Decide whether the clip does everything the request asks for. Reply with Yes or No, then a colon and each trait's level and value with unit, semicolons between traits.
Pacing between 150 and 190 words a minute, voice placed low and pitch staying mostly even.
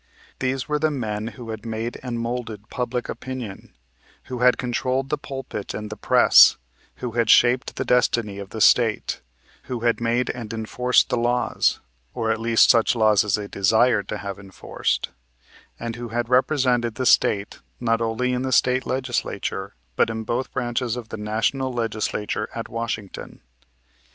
Yes: average, 165 wpm; low, 120 Hz; narrow, 2.3 semitones